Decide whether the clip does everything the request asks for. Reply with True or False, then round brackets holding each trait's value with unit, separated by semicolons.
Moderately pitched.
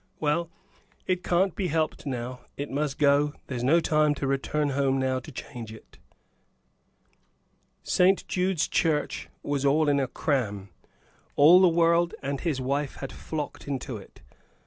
True (145 Hz)